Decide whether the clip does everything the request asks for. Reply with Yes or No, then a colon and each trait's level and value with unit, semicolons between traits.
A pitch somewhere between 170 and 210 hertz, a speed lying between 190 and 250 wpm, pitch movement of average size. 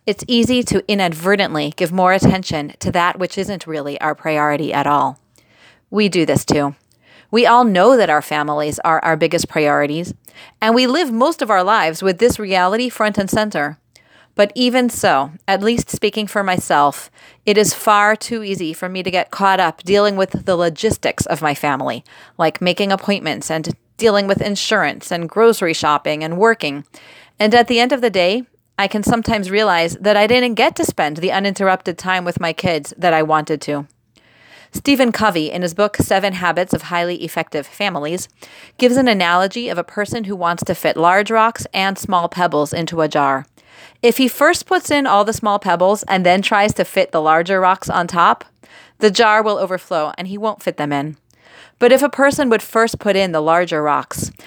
Yes: medium, 185 Hz; average, 195 wpm; average, 5.0 semitones